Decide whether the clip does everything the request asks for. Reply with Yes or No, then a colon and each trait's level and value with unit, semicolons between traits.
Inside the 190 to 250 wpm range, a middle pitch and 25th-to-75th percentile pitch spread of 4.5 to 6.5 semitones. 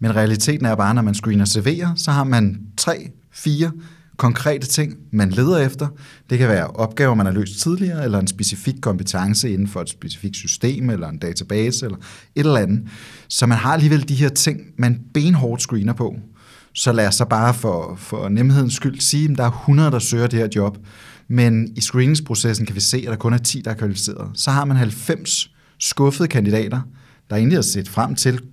No: average, 210 wpm; low, 120 Hz; average, 4.9 semitones